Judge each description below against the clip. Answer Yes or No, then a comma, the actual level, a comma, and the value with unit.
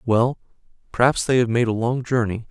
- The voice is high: No, low, 120 Hz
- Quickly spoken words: No, average, 190 wpm